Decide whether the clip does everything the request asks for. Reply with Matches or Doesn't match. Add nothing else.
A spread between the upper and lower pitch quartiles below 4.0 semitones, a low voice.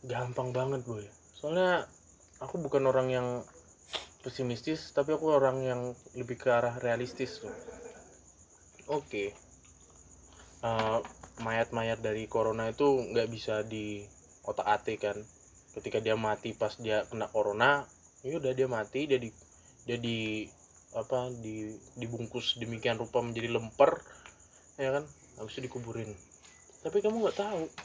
Matches